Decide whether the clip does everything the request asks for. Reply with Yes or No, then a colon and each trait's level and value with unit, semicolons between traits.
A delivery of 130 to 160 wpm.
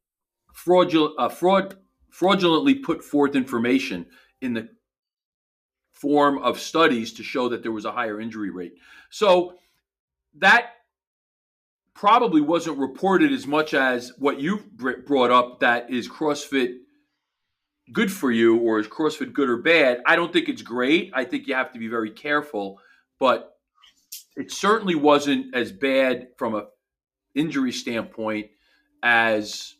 Yes: average, 140 wpm